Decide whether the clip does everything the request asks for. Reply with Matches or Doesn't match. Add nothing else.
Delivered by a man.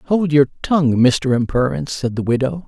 Matches